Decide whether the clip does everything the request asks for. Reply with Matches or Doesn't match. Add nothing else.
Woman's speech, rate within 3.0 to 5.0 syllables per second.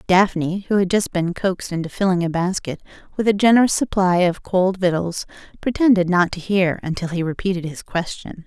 Doesn't match